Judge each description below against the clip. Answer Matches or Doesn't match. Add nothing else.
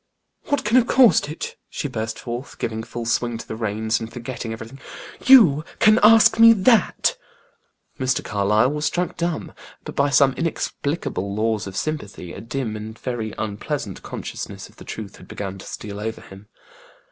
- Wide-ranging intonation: Matches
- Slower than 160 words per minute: Doesn't match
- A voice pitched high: Doesn't match